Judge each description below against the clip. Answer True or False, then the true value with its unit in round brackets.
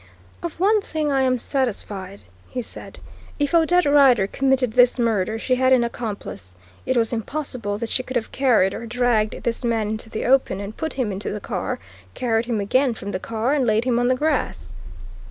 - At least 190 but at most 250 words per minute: True (200 wpm)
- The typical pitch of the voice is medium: False (240 Hz)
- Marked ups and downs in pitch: False (3.5 semitones)